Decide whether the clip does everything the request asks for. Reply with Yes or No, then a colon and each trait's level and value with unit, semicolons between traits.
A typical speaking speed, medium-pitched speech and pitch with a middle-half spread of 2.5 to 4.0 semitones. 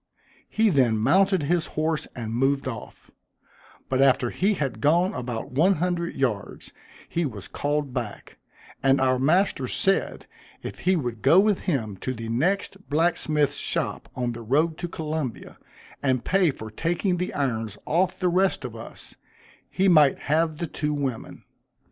No: average, 160 wpm; medium, 145 Hz; wide, 5.6 semitones